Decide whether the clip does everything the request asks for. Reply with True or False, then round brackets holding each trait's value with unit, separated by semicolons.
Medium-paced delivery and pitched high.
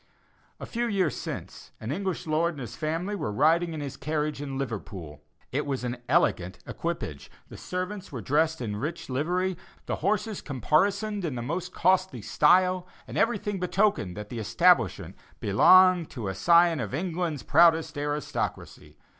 False (160 wpm; 160 Hz)